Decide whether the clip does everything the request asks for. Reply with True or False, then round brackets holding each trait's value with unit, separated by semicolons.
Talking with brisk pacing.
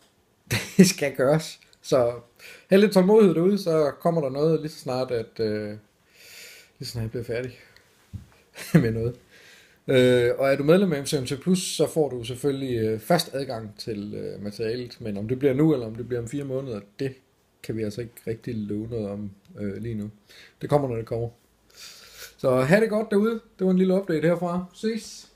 False (200 wpm)